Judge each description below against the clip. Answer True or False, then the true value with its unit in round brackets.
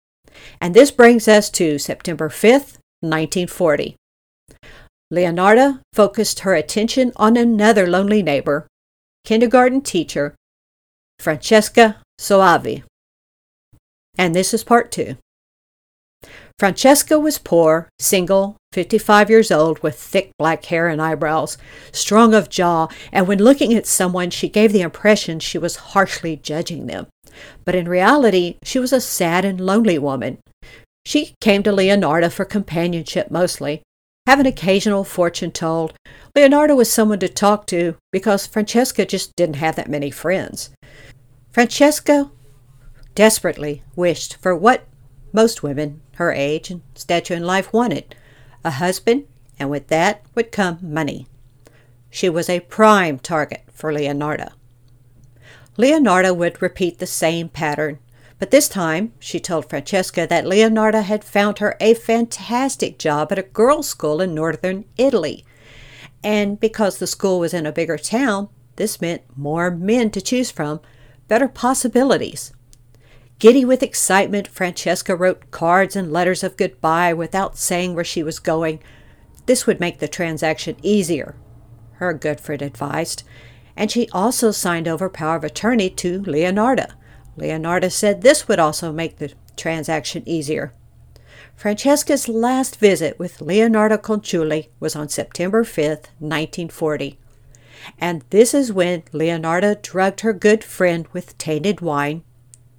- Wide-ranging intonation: True (5.7 semitones)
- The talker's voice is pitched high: False (175 Hz)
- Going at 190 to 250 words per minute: False (135 wpm)